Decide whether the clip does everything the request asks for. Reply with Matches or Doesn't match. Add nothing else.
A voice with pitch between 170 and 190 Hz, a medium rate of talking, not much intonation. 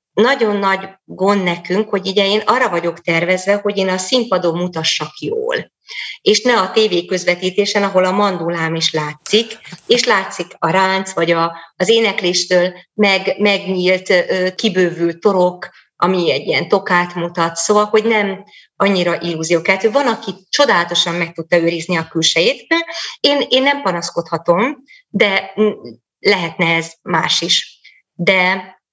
Doesn't match